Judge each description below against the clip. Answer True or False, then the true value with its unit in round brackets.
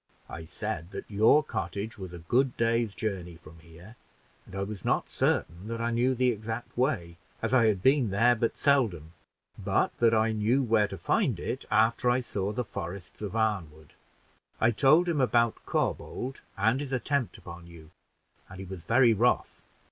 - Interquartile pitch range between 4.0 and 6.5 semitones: True (4.7 semitones)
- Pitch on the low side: True (110 Hz)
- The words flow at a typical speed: True (180 wpm)